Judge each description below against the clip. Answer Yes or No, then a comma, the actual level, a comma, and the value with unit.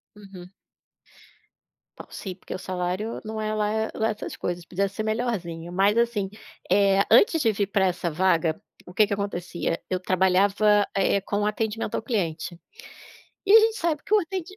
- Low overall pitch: No, high, 200 Hz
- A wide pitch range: No, average, 3.2 semitones